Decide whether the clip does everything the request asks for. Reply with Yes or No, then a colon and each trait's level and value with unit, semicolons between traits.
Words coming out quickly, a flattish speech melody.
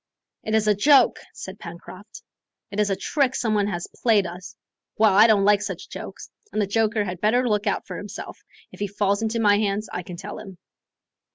Yes: fast, 210 wpm; narrow, 1.8 semitones